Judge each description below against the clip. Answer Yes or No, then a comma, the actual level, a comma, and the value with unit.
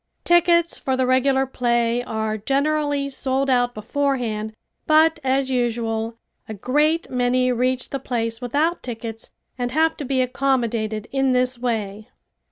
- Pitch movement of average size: Yes, average, 3.0 semitones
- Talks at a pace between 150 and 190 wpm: No, average, 140 wpm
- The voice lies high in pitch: Yes, very high, 255 Hz